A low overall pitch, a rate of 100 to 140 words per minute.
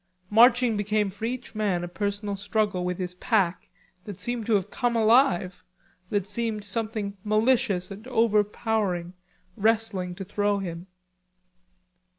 No: high, 205 Hz; slow, 135 wpm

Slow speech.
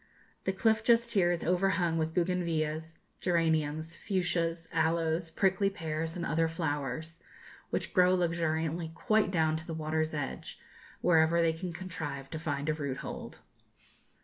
No: average, 145 wpm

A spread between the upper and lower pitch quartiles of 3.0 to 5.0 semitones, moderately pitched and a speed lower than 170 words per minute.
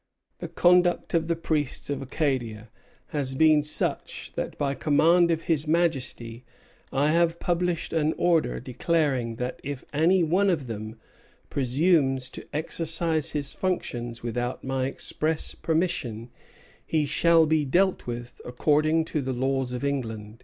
Yes: average, 4.6 semitones; medium, 150 Hz; average, 140 wpm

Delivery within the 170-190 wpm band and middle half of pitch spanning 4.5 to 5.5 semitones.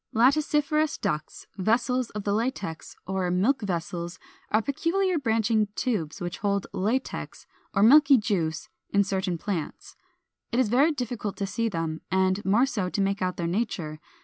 No: average, 160 wpm; average, 5.2 semitones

